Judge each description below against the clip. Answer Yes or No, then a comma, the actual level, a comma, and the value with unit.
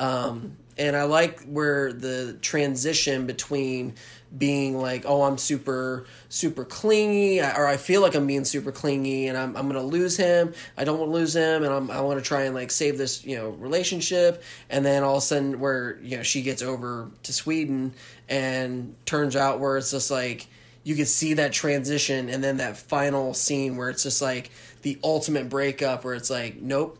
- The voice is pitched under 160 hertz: Yes, low, 135 Hz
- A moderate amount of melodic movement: No, narrow, 2.2 semitones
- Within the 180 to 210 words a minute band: Yes, average, 200 wpm